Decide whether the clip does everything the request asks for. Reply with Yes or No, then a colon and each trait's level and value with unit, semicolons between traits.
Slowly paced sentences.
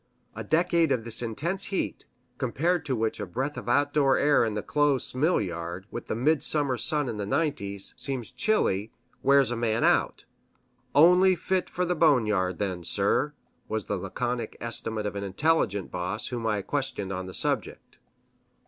No: average, 170 wpm